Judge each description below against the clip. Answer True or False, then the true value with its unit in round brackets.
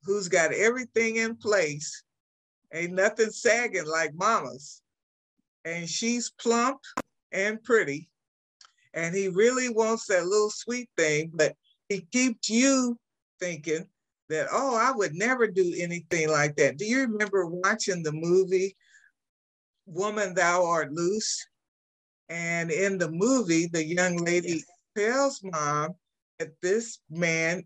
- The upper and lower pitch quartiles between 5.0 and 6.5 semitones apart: True (5.3 semitones)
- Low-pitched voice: False (185 Hz)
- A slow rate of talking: True (130 wpm)